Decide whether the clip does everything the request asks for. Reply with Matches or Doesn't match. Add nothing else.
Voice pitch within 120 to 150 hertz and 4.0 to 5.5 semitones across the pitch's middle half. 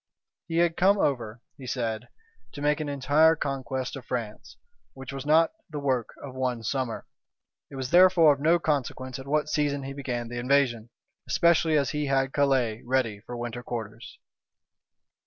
Doesn't match